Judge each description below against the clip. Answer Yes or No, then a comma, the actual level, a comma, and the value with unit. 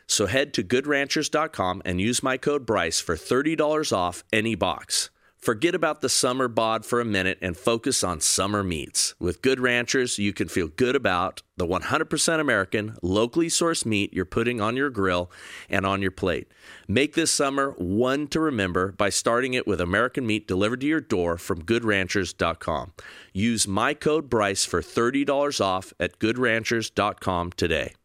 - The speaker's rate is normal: Yes, average, 165 wpm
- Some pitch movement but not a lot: No, wide, 5.8 semitones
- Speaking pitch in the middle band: No, low, 110 Hz